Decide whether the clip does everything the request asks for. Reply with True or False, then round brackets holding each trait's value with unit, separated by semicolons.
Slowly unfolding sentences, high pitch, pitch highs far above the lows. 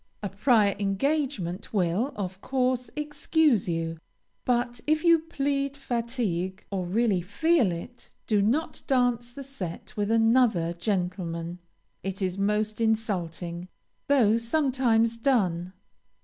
True (120 wpm; 225 Hz; 5.7 semitones)